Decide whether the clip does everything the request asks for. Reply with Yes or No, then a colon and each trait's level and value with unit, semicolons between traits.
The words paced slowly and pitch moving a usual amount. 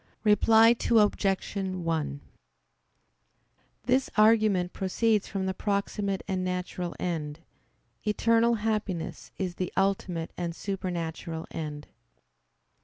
Yes: slow, 95 wpm; average, 3.4 semitones